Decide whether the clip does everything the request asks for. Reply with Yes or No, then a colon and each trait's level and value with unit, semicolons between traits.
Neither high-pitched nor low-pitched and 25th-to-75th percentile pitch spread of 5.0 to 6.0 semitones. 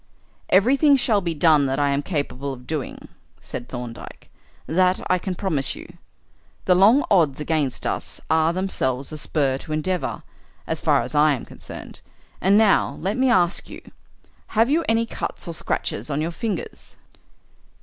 Yes: medium, 165 Hz; wide, 5.6 semitones